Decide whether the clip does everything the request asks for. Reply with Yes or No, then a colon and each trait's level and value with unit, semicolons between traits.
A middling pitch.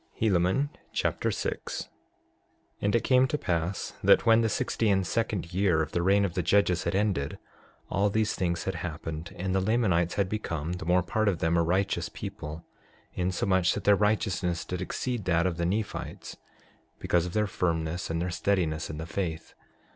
No: very low, 90 Hz